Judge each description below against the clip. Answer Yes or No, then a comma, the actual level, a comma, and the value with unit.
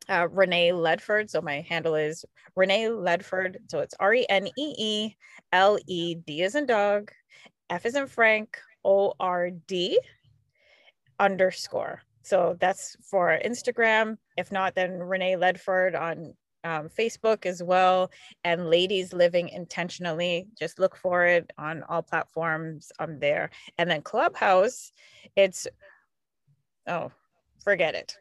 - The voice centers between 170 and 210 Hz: Yes, medium, 185 Hz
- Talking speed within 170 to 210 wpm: No, slow, 135 wpm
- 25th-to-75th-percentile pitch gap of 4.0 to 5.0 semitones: No, average, 2.9 semitones